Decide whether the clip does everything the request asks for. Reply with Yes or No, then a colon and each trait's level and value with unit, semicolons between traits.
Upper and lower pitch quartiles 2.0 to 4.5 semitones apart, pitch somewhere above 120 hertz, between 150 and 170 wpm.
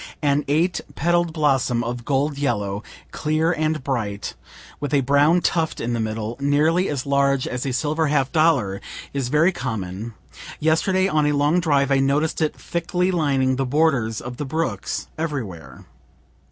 Yes: average, 4.2 semitones; medium, 140 Hz; average, 160 wpm